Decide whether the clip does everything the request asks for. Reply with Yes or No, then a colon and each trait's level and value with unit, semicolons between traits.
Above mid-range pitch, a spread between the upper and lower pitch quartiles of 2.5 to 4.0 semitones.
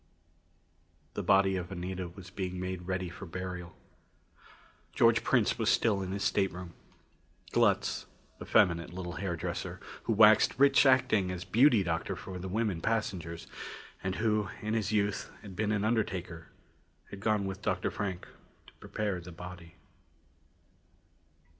No: very low, 95 Hz; average, 2.9 semitones